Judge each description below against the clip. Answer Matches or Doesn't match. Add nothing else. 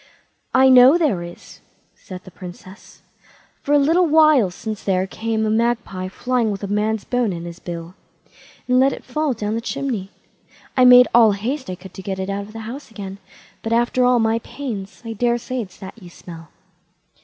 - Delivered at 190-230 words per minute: Matches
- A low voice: Doesn't match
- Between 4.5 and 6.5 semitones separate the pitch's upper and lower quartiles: Matches